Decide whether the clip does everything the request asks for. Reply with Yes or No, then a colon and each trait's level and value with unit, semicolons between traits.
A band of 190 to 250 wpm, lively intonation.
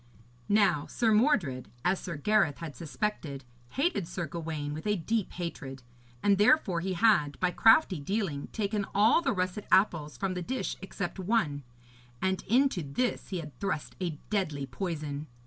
No: average, 160 wpm; wide, 5.8 semitones